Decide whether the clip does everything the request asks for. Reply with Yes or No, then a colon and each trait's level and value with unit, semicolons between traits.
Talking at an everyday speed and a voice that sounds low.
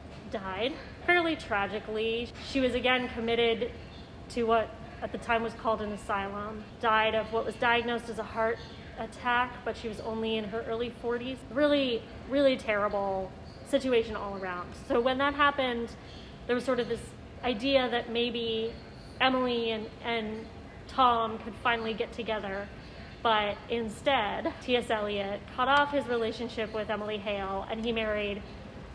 No: average, 150 wpm; high, 230 Hz